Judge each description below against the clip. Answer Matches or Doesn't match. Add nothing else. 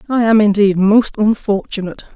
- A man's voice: Doesn't match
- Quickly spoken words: Doesn't match